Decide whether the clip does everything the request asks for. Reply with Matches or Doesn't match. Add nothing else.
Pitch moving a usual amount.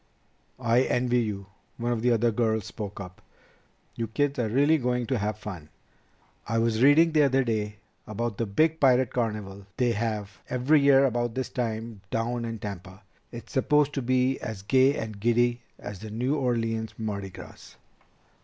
Matches